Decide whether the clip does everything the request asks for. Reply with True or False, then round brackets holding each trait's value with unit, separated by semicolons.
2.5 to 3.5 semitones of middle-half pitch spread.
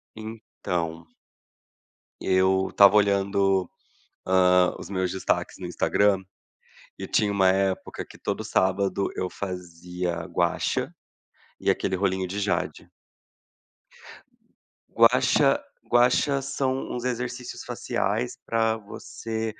True (3.1 semitones)